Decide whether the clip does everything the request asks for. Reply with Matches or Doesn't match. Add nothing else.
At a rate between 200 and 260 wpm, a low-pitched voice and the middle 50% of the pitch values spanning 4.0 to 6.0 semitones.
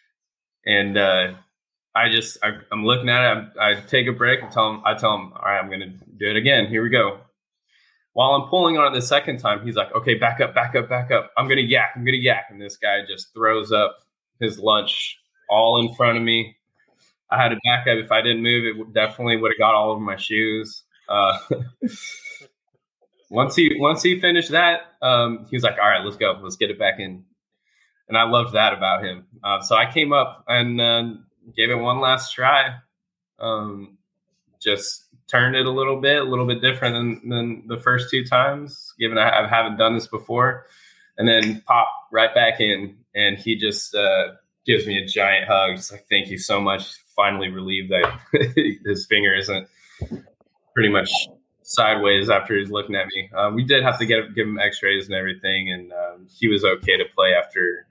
Doesn't match